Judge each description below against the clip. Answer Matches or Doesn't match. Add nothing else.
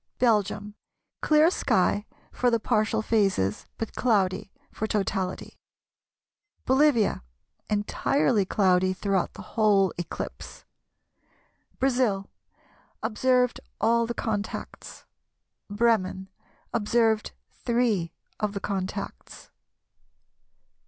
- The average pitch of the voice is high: Matches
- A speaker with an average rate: Doesn't match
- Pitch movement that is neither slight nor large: Matches